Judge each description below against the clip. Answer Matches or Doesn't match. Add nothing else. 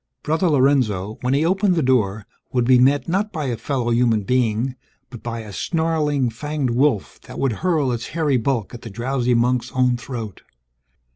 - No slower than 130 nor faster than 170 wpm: Doesn't match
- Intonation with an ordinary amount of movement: Matches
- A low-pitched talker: Matches